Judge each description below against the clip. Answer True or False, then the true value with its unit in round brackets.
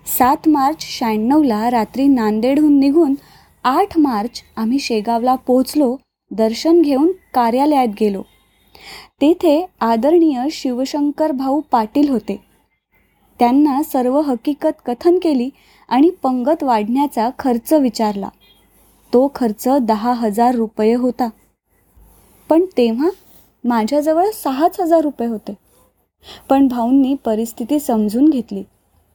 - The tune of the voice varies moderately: True (4.2 semitones)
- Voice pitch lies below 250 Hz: False (260 Hz)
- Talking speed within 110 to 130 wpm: False (100 wpm)